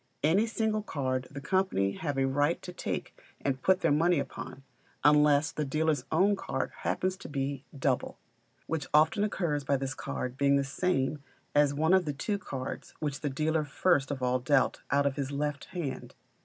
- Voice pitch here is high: No, medium, 145 Hz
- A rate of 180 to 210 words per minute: Yes, average, 185 wpm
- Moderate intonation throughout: Yes, average, 3.3 semitones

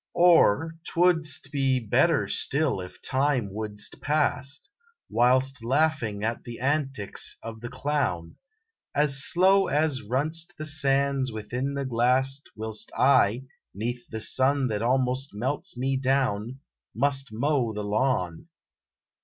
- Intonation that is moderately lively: Yes, average, 3.9 semitones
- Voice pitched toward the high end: No, low, 130 Hz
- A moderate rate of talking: No, slow, 125 wpm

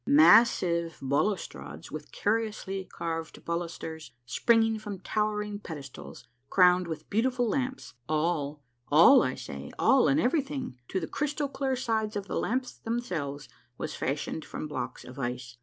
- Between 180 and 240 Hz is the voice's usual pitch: Yes, high, 190 Hz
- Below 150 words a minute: Yes, average, 140 wpm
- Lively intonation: Yes, wide, 7.0 semitones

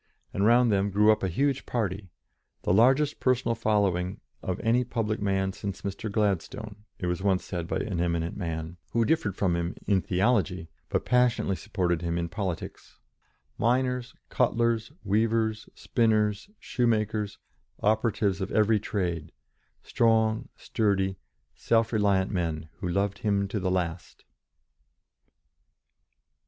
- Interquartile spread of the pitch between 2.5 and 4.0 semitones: Yes, average, 3.5 semitones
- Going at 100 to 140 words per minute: Yes, slow, 135 wpm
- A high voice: No, low, 100 Hz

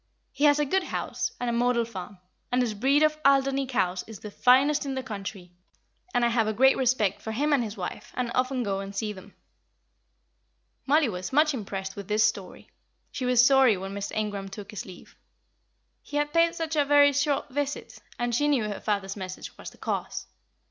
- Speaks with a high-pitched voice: Yes, high, 245 Hz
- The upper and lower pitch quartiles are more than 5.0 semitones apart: Yes, wide, 5.5 semitones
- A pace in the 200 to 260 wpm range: Yes, fast, 205 wpm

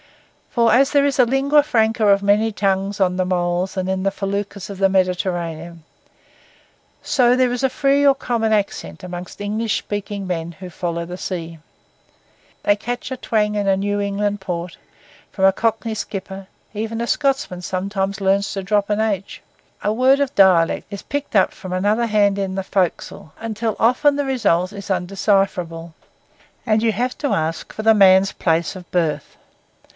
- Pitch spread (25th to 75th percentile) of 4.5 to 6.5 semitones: No, average, 3.3 semitones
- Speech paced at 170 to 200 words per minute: Yes, average, 180 wpm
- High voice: Yes, high, 200 Hz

